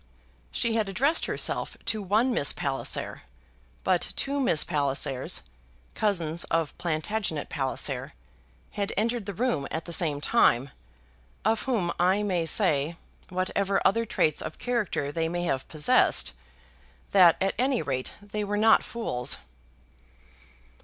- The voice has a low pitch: No, medium, 185 Hz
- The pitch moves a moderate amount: No, wide, 6.0 semitones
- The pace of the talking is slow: Yes, slow, 130 wpm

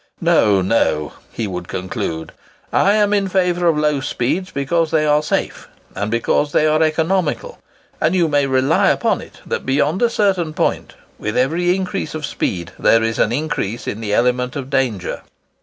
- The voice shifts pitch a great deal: Yes, wide, 6.6 semitones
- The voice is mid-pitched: Yes, medium, 145 Hz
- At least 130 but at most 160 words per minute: No, average, 175 wpm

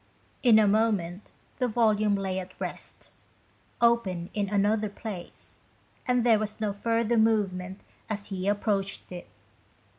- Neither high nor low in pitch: No, high, 210 Hz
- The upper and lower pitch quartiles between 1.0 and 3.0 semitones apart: Yes, narrow, 2.4 semitones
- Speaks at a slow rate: Yes, slow, 130 wpm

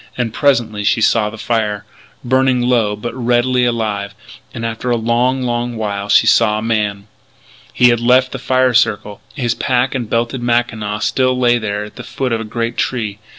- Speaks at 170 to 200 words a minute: Yes, average, 190 wpm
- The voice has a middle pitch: No, low, 120 Hz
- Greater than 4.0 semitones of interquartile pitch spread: No, narrow, 2.5 semitones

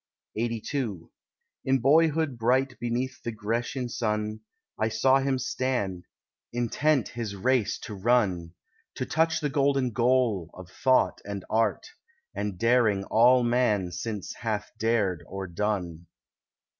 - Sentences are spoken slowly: Yes, slow, 125 wpm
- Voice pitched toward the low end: Yes, low, 115 Hz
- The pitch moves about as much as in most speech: Yes, average, 4.0 semitones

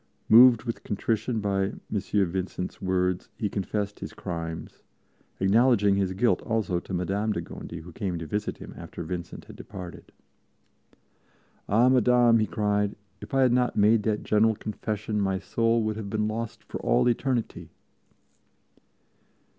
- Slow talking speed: No, average, 150 wpm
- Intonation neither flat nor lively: Yes, average, 3.0 semitones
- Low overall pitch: Yes, low, 105 Hz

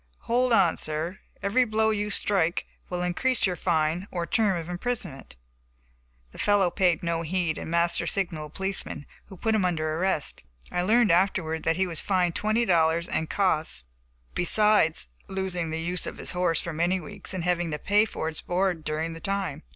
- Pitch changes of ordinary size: Yes, average, 3.3 semitones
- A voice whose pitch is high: No, medium, 180 Hz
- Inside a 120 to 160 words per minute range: No, average, 185 wpm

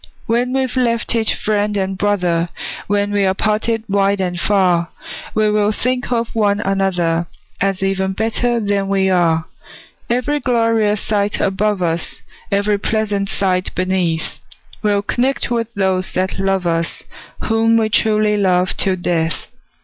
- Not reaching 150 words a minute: Yes, average, 140 wpm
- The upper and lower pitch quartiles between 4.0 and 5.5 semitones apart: No, average, 2.8 semitones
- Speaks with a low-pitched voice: No, high, 200 Hz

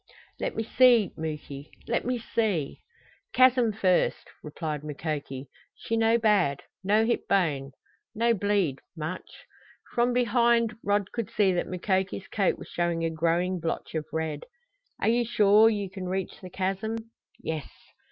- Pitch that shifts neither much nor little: No, wide, 5.7 semitones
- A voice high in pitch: Yes, high, 195 Hz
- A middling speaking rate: Yes, average, 150 wpm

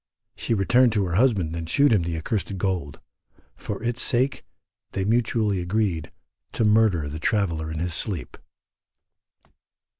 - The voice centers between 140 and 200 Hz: No, low, 100 Hz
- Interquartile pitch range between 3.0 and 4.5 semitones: No, average, 5.2 semitones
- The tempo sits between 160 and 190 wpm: No, average, 145 wpm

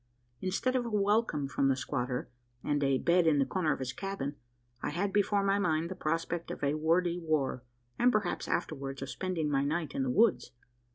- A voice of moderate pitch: Yes, medium, 160 Hz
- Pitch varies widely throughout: Yes, wide, 5.7 semitones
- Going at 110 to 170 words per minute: No, fast, 205 wpm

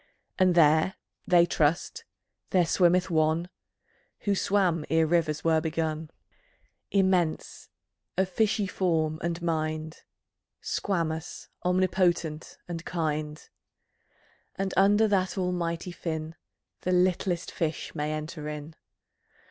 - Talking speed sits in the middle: No, slow, 105 wpm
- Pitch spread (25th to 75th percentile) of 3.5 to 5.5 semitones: No, average, 2.7 semitones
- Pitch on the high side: No, medium, 170 Hz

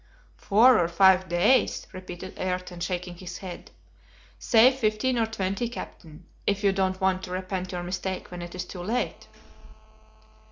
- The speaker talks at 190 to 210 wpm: No, average, 155 wpm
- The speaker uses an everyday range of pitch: No, narrow, 2.3 semitones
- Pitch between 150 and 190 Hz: Yes, medium, 185 Hz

